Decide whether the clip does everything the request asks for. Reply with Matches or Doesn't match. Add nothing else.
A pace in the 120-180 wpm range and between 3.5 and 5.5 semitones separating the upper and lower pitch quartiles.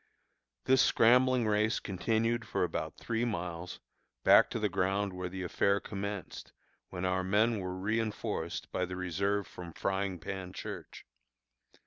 Doesn't match